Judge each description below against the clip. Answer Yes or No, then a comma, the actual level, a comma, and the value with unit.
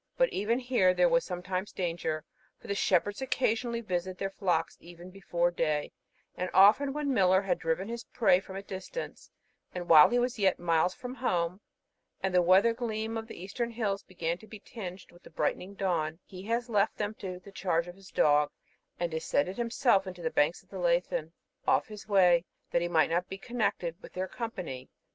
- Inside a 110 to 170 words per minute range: No, average, 200 wpm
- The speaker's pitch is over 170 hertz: Yes, high, 190 Hz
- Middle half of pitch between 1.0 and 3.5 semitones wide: No, average, 4.2 semitones